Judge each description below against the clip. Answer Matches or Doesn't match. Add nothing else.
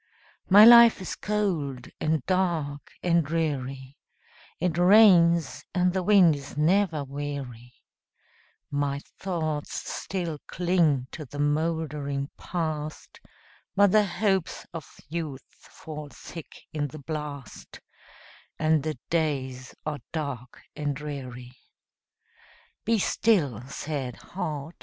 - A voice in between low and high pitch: Matches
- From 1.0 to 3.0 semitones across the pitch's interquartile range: Doesn't match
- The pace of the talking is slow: Matches